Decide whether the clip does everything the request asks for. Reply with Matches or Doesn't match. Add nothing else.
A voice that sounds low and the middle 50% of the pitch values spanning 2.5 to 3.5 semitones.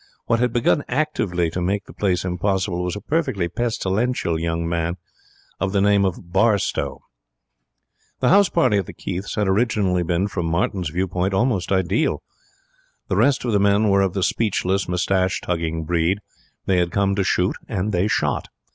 Matches